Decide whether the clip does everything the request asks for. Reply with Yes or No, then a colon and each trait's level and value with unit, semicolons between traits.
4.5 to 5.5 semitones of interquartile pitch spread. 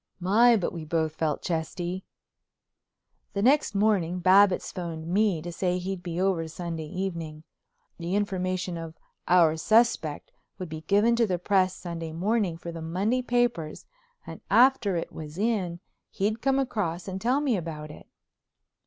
No: average, 3.9 semitones